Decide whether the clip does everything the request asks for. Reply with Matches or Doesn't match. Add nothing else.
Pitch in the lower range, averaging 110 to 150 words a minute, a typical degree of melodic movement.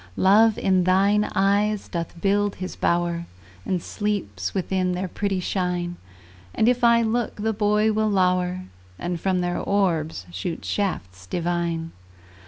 Doesn't match